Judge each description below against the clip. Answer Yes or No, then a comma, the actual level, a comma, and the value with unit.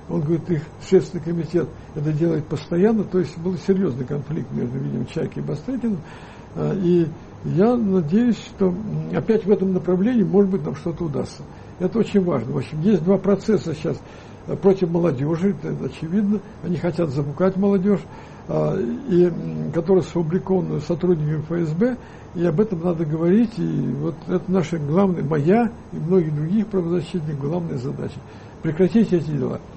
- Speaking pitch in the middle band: Yes, medium, 175 Hz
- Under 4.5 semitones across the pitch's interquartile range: Yes, average, 3.6 semitones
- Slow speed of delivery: No, average, 145 wpm